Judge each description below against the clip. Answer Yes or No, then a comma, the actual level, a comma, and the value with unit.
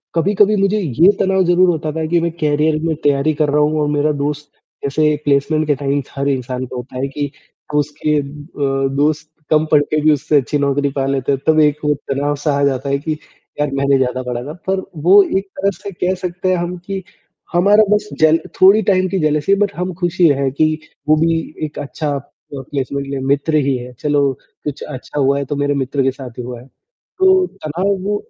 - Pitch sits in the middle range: Yes, medium, 150 Hz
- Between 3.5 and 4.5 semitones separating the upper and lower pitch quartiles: Yes, average, 3.8 semitones